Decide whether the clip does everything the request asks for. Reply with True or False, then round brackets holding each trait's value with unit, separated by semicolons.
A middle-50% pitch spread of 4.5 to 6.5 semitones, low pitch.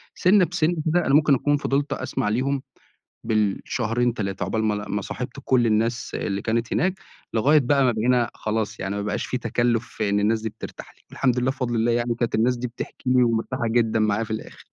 False (2.9 semitones; 120 Hz)